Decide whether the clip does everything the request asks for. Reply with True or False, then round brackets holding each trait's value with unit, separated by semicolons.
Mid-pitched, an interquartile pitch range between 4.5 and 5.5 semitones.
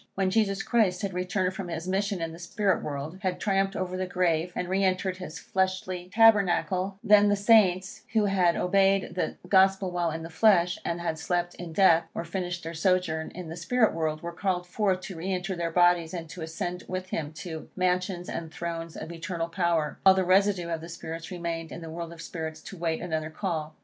False (180 Hz; 2.4 semitones)